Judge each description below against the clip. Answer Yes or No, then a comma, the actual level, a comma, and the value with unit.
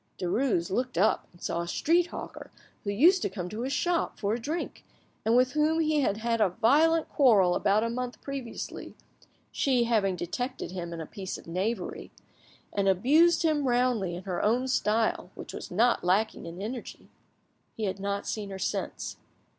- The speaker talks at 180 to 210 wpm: Yes, average, 185 wpm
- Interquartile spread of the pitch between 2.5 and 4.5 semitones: No, wide, 5.4 semitones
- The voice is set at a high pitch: Yes, high, 225 Hz